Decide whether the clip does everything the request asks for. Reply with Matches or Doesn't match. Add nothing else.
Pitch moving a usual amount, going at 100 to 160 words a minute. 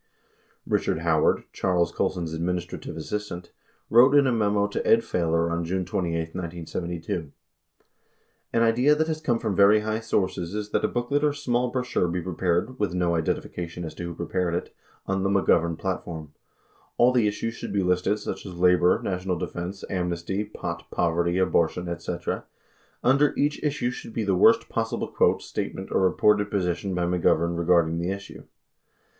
Doesn't match